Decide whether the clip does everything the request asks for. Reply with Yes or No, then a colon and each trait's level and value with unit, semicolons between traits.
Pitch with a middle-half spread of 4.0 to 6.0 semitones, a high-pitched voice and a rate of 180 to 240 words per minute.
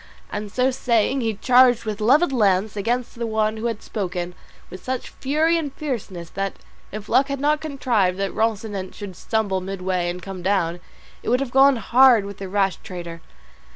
Yes: average, 4.8 semitones; high, 215 Hz; average, 185 wpm